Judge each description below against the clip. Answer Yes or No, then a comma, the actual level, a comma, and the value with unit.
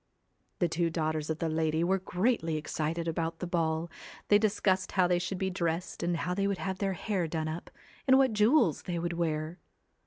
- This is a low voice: No, medium, 175 Hz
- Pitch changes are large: No, average, 2.8 semitones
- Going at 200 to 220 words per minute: Yes, fast, 205 wpm